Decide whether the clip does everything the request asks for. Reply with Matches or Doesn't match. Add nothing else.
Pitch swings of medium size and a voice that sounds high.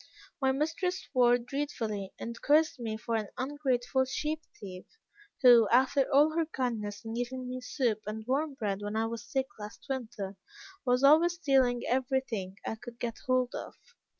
Matches